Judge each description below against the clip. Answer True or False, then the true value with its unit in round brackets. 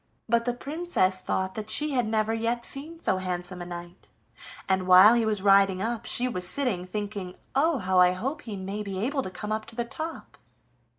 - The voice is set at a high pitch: True (215 Hz)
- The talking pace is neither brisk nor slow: False (210 wpm)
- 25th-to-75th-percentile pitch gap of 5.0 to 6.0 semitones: False (4.5 semitones)